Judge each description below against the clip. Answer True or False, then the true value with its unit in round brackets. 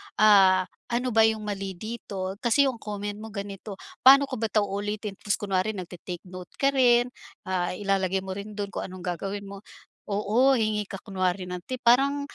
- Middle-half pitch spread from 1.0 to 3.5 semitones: True (2.9 semitones)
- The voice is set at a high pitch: True (205 Hz)